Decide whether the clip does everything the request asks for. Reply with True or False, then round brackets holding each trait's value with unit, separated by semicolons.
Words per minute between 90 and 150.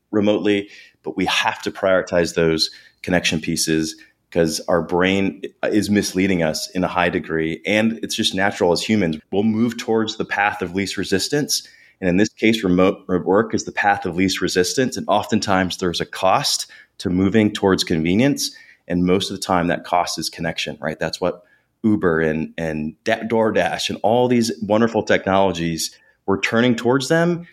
False (170 wpm)